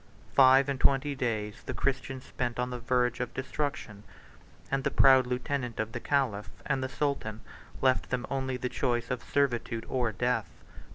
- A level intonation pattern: Yes, narrow, 2.0 semitones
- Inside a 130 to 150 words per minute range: No, average, 170 wpm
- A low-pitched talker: Yes, low, 125 Hz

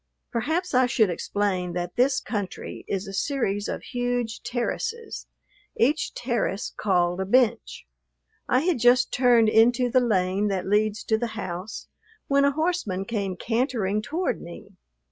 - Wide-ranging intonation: No, average, 4.5 semitones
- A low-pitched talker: No, high, 225 Hz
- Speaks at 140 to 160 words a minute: Yes, average, 145 wpm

